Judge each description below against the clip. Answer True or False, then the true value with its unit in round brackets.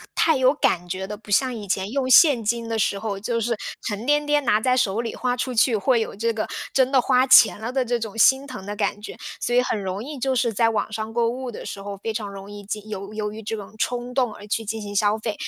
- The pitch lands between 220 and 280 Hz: True (225 Hz)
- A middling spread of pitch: True (3.3 semitones)